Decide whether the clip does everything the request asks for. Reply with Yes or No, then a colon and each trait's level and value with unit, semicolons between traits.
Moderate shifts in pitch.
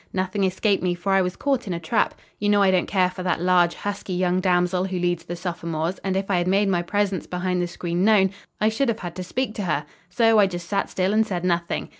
No: narrow, 2.2 semitones